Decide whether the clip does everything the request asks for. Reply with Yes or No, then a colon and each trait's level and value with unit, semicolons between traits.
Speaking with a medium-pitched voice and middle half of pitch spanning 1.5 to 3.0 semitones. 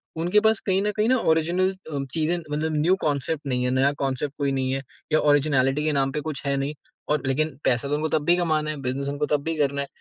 Yes: medium, 150 Hz; average, 2.7 semitones